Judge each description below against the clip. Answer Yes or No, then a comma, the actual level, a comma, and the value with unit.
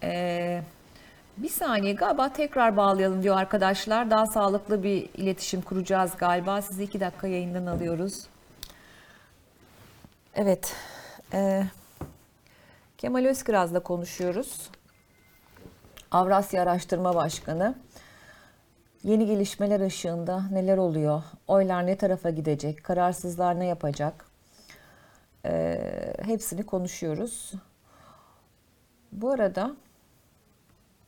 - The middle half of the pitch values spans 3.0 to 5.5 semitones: No, narrow, 2.5 semitones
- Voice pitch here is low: No, high, 190 Hz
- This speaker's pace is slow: Yes, slow, 85 wpm